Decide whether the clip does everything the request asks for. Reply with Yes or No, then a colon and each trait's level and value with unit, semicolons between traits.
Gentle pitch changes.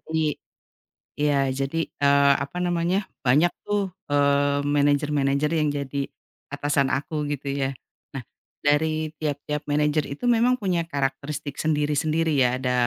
Yes: narrow, 1.7 semitones